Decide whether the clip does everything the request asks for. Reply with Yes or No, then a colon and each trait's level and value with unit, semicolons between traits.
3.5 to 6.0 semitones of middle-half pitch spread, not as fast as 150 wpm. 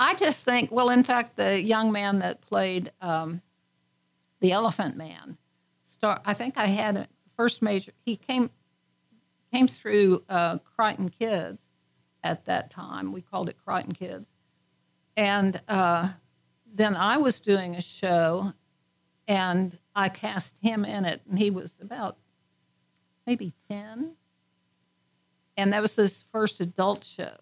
Yes: average, 4.6 semitones; average, 140 wpm